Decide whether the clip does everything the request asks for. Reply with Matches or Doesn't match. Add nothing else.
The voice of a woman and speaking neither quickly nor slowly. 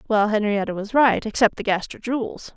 Matches